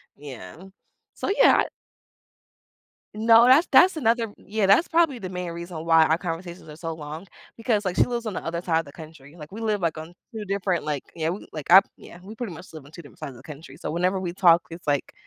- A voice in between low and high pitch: Yes, medium, 175 Hz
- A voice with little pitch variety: No, average, 4.8 semitones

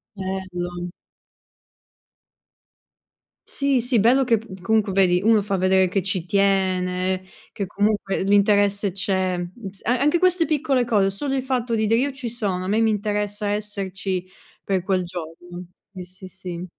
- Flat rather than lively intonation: No, average, 3.3 semitones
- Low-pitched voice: No, high, 195 Hz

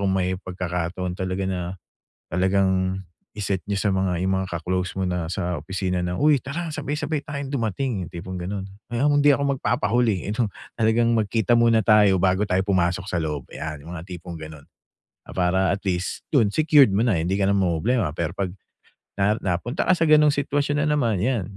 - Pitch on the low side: Yes, very low, 95 Hz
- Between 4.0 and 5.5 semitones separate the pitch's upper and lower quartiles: Yes, average, 4.8 semitones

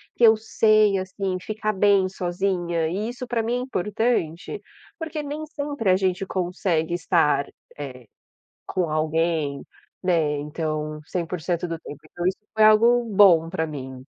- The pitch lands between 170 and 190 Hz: Yes, medium, 185 Hz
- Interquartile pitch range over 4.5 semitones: Yes, average, 5.0 semitones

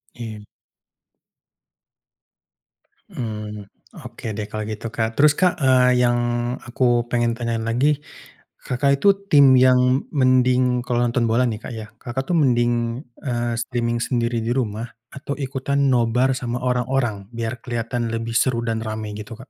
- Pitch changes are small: Yes, narrow, 2.0 semitones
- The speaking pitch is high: No, low, 120 Hz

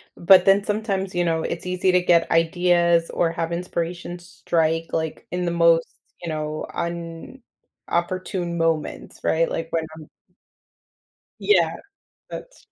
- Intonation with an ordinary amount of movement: No, narrow, 1.6 semitones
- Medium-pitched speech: Yes, medium, 170 Hz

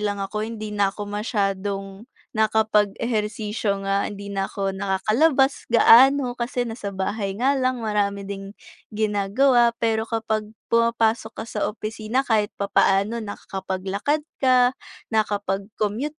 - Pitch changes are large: No, average, 2.7 semitones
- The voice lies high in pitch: Yes, high, 215 Hz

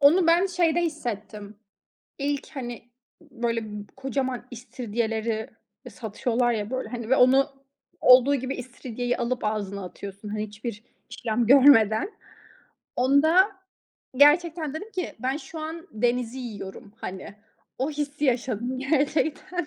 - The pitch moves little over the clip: No, average, 4.5 semitones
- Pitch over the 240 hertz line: Yes, very high, 250 Hz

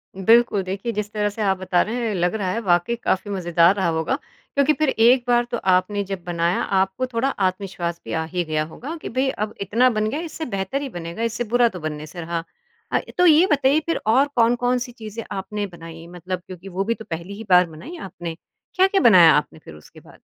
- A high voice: Yes, high, 200 Hz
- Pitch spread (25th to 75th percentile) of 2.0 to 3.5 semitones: No, wide, 5.5 semitones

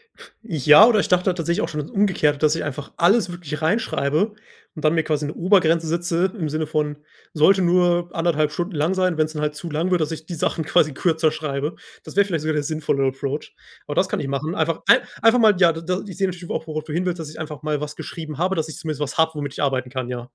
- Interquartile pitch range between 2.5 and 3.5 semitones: Yes, average, 2.8 semitones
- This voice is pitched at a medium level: Yes, medium, 160 Hz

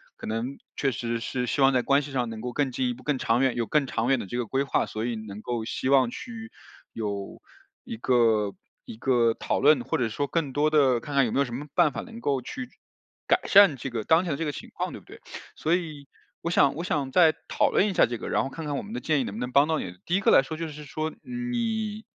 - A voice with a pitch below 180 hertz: Yes, low, 135 Hz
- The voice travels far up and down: No, average, 4.8 semitones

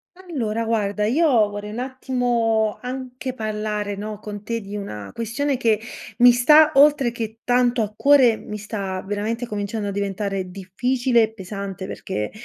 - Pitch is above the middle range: Yes, high, 220 Hz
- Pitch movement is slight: No, average, 3.3 semitones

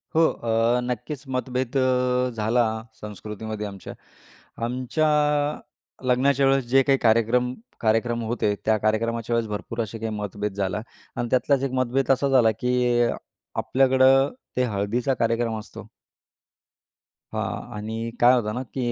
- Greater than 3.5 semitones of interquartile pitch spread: No, average, 2.8 semitones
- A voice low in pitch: Yes, low, 120 Hz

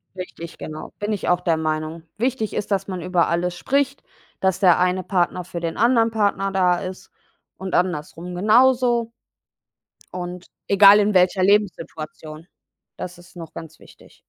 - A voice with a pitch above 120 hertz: Yes, medium, 185 Hz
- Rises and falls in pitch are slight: No, average, 3.1 semitones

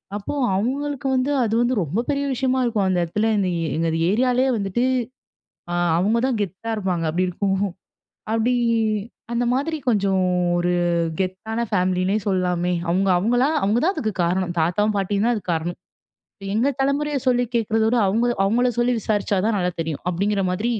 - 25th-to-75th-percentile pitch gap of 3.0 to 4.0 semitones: No, average, 4.8 semitones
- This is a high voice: Yes, high, 210 Hz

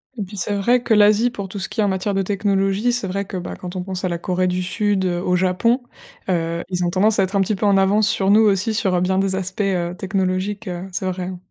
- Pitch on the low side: No, high, 195 Hz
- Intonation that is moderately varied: No, narrow, 2.1 semitones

